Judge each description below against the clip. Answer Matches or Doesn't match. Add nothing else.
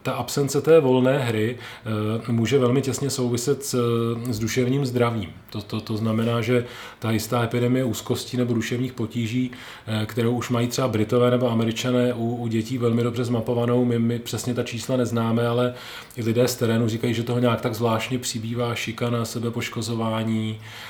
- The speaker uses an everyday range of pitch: Doesn't match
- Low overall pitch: Matches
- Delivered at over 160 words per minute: Matches